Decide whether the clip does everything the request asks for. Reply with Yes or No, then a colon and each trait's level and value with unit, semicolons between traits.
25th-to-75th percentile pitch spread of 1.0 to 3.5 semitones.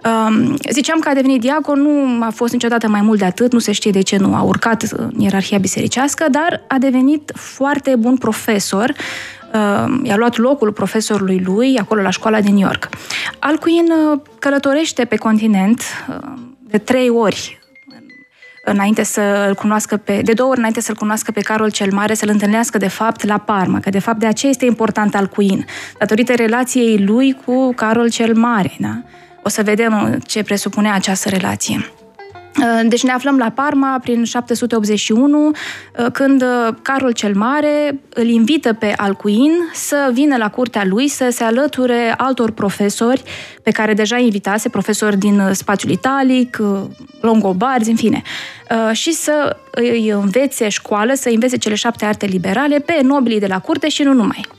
No: average, 3.9 semitones